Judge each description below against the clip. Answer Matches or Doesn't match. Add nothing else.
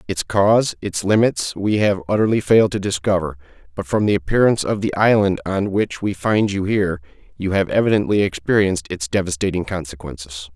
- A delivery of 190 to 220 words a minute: Doesn't match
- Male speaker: Matches